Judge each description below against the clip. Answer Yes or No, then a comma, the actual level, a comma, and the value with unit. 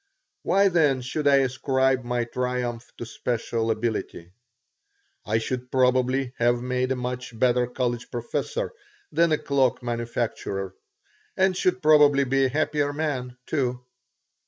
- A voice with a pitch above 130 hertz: No, low, 125 Hz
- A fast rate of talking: No, slow, 135 wpm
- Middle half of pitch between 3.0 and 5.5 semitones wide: No, narrow, 2.6 semitones